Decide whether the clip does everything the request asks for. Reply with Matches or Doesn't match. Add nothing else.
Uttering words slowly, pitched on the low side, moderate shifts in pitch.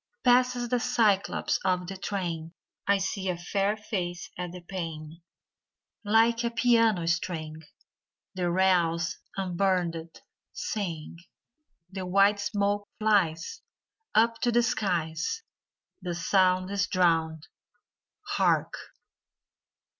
Doesn't match